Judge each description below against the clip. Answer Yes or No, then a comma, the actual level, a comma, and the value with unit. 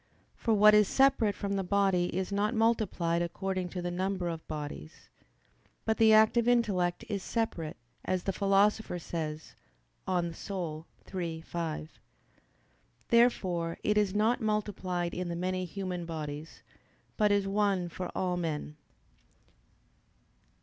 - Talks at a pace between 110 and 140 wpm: Yes, slow, 135 wpm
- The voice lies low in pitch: No, medium, 185 Hz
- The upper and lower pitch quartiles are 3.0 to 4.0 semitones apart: Yes, average, 3.5 semitones